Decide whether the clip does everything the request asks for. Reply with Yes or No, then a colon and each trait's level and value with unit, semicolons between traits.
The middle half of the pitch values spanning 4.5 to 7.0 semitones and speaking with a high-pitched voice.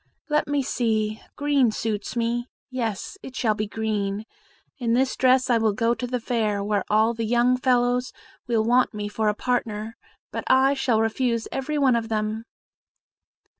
No: average, 2.7 semitones; high, 230 Hz